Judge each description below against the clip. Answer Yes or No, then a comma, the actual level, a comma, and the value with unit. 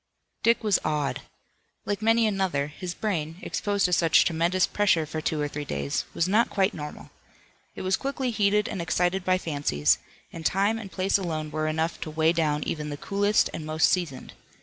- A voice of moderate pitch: Yes, medium, 170 Hz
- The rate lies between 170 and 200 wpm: Yes, average, 190 wpm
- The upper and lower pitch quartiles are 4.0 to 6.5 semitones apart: Yes, average, 4.4 semitones